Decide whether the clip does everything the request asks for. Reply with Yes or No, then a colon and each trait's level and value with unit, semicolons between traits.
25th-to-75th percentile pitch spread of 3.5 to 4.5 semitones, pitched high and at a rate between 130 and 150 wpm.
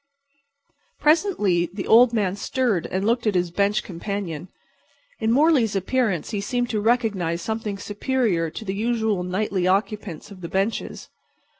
Yes: average, 3.8 semitones; high, 205 Hz; average, 145 wpm